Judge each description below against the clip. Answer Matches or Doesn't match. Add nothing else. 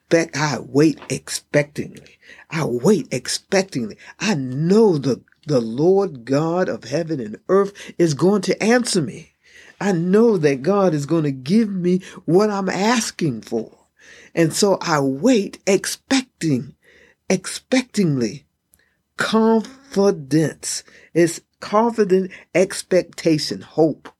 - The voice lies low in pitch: Doesn't match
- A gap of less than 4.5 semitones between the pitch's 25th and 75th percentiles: Doesn't match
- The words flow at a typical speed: Doesn't match